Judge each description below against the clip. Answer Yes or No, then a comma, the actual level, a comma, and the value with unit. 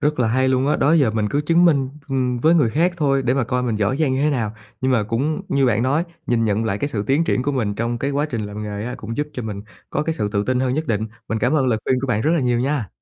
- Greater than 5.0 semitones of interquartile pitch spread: No, average, 4.2 semitones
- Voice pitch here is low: Yes, low, 130 Hz